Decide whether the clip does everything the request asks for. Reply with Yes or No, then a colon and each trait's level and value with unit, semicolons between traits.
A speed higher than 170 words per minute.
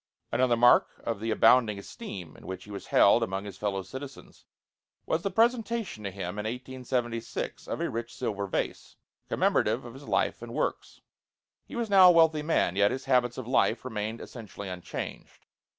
Yes: average, 180 wpm